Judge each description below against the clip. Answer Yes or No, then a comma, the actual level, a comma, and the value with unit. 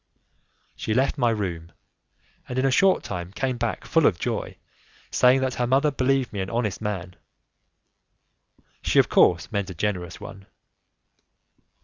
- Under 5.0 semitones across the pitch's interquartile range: No, wide, 5.6 semitones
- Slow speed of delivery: No, average, 150 wpm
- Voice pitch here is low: Yes, low, 110 Hz